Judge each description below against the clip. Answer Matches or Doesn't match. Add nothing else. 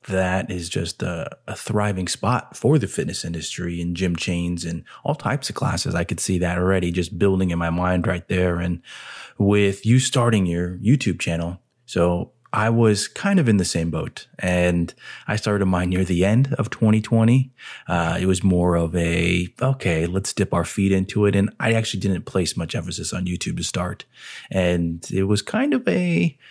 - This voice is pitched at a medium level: Doesn't match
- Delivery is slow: Doesn't match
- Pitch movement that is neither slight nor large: Matches